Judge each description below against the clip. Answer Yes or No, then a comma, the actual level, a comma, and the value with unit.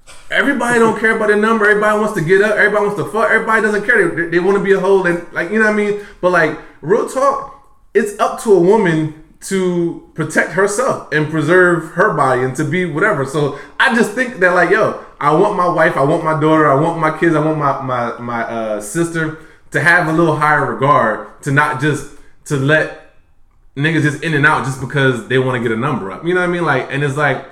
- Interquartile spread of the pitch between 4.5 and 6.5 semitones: Yes, wide, 5.6 semitones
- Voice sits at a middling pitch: Yes, medium, 160 Hz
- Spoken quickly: Yes, fast, 245 wpm